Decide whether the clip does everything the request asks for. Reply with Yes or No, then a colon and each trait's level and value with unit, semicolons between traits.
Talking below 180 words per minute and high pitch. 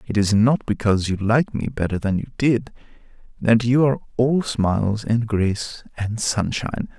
No: average, 170 wpm; low, 115 Hz